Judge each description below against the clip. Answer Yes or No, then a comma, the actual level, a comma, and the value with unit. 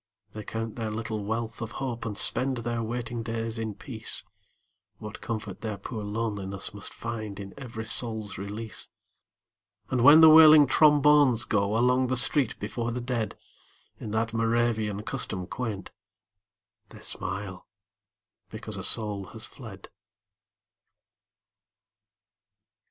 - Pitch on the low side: Yes, low, 115 Hz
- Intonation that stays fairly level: Yes, narrow, 2.3 semitones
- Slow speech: Yes, slow, 130 wpm